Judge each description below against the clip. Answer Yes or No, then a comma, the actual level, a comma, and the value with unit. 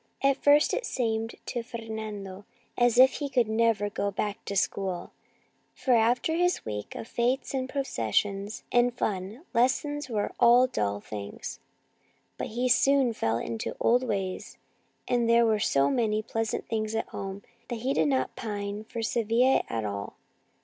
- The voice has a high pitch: Yes, high, 225 Hz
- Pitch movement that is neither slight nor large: Yes, average, 3.7 semitones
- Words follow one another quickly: No, average, 165 wpm